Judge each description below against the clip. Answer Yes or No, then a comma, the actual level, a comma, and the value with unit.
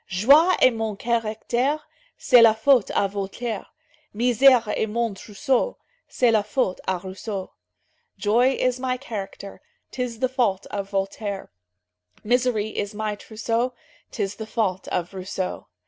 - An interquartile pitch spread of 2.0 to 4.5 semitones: Yes, average, 3.7 semitones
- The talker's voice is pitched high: Yes, high, 220 Hz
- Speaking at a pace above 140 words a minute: No, slow, 135 wpm